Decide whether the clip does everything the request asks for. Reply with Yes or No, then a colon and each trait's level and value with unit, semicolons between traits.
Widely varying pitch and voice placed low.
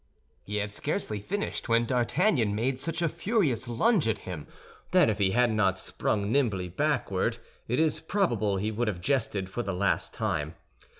Yes: wide, 6.1 semitones; low, 115 Hz